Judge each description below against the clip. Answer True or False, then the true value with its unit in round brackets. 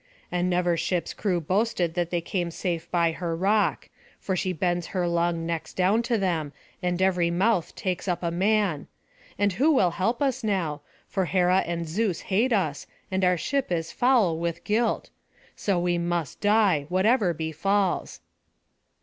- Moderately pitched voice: True (180 Hz)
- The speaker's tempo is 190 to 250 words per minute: False (165 wpm)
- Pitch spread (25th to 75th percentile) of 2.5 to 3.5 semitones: True (3.0 semitones)